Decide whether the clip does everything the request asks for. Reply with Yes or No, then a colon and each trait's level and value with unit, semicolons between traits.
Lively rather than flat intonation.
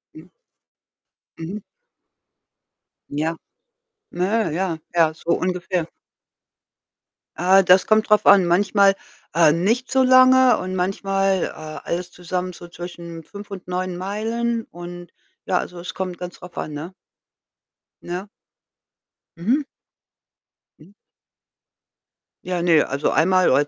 No: narrow, 2.5 semitones